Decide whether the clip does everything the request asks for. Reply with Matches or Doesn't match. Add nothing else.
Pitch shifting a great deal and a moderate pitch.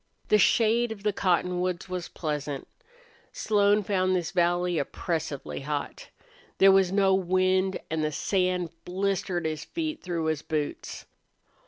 Doesn't match